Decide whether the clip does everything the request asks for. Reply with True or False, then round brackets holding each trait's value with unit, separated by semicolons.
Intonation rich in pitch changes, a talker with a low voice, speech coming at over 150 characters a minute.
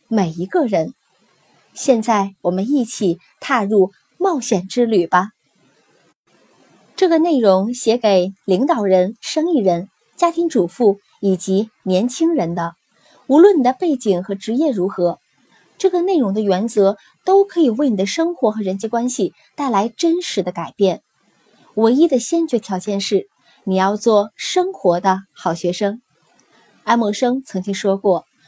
False (6.4 semitones; 215 Hz; 215 characters per minute)